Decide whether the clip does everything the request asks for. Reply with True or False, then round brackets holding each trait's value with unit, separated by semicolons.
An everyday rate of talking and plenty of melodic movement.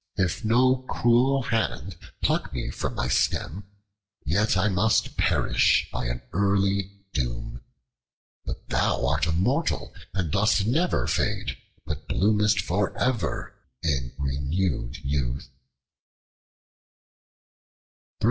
False (105 wpm; 7.1 semitones)